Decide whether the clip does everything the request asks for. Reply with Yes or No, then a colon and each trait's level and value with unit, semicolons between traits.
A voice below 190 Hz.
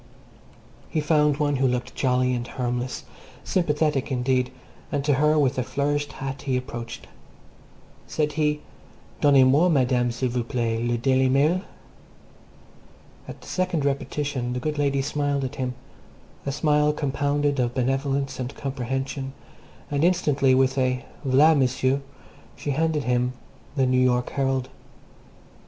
Yes: low, 135 Hz